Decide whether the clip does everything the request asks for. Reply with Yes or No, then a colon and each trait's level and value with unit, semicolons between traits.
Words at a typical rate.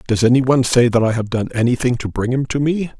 No: fast, 280 wpm